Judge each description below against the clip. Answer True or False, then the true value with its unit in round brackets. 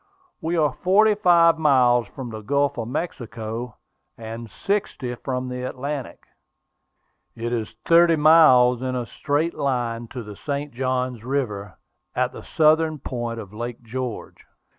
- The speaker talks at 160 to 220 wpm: False (140 wpm)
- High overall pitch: False (125 Hz)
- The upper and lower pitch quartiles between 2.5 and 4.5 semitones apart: True (4.2 semitones)